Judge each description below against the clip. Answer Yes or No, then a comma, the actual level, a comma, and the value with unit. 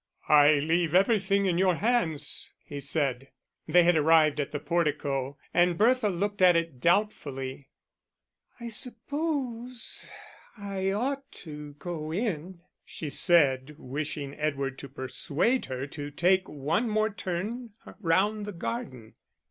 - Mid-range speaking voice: Yes, medium, 170 Hz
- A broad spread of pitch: Yes, wide, 6.0 semitones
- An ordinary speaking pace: No, slow, 130 wpm